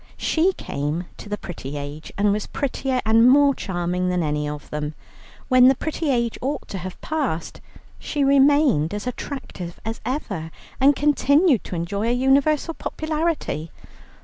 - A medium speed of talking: Yes, average, 155 wpm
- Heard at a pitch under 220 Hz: No, high, 235 Hz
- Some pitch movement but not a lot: No, wide, 8.4 semitones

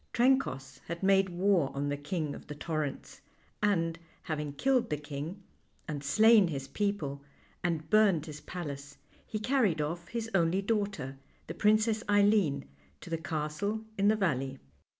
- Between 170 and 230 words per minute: No, average, 150 wpm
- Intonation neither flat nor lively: No, wide, 5.8 semitones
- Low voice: No, medium, 170 Hz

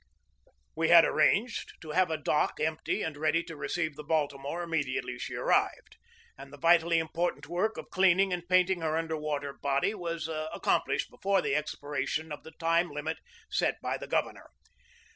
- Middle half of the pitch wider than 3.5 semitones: No, narrow, 2.4 semitones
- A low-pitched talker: No, medium, 160 Hz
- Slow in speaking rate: No, average, 175 wpm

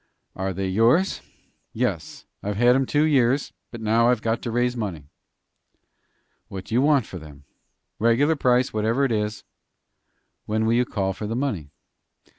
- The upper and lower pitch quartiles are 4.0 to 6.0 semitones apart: No, average, 3.3 semitones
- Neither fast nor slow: Yes, average, 165 wpm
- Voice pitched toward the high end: No, low, 115 Hz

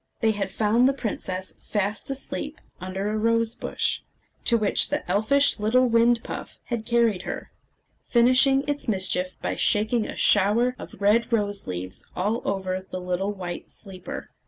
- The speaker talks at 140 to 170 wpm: Yes, average, 160 wpm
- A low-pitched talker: No, high, 215 Hz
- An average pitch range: Yes, average, 3.7 semitones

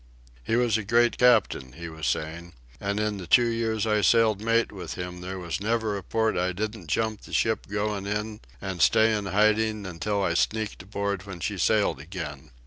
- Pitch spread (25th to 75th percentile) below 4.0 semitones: Yes, average, 3.4 semitones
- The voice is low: Yes, low, 105 Hz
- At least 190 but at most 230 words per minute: Yes, average, 200 wpm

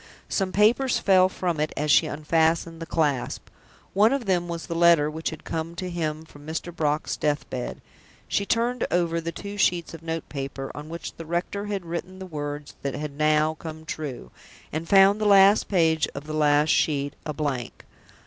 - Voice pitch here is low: No, medium, 165 Hz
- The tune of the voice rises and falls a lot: No, average, 3.4 semitones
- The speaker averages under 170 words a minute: No, average, 195 wpm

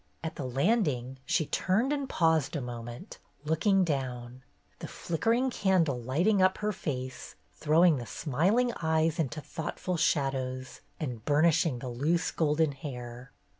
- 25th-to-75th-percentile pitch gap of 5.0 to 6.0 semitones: Yes, wide, 5.4 semitones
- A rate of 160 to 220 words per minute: No, slow, 135 wpm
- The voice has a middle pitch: Yes, medium, 155 Hz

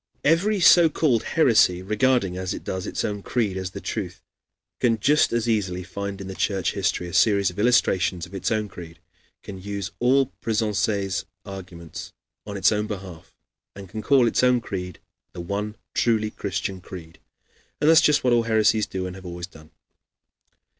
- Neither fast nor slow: Yes, average, 180 wpm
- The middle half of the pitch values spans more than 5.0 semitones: No, average, 3.8 semitones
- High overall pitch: No, low, 100 Hz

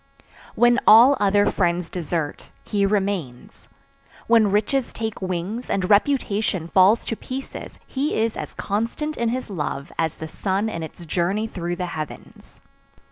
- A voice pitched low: No, high, 200 Hz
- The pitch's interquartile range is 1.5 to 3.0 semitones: No, average, 4.6 semitones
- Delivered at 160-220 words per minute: No, average, 145 wpm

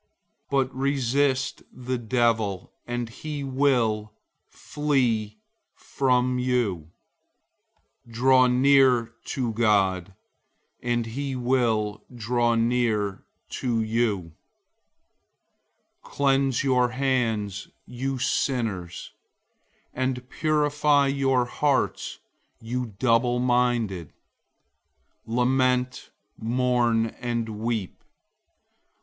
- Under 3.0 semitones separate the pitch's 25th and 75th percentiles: Yes, narrow, 2.6 semitones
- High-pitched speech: No, low, 125 Hz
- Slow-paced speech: Yes, slow, 80 wpm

